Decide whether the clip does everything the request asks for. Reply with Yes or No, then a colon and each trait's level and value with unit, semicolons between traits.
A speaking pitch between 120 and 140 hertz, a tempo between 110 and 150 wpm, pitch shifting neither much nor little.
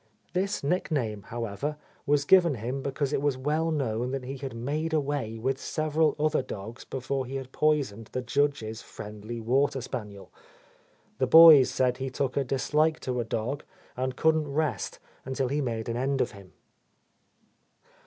No: low, 135 Hz; average, 165 wpm; average, 3.6 semitones